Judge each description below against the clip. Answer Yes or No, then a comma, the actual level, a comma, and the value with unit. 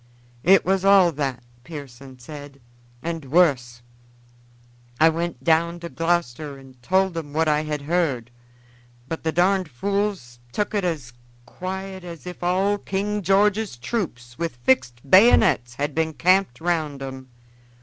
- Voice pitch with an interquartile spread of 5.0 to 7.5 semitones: Yes, wide, 5.6 semitones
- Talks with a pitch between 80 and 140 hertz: No, medium, 160 Hz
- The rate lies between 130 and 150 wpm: Yes, average, 140 wpm